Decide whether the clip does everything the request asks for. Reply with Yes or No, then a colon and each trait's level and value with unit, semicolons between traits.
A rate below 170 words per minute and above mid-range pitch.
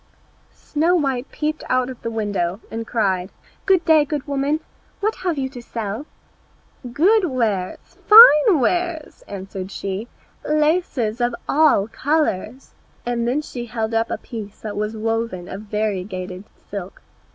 Yes: average, 140 wpm; high, 240 Hz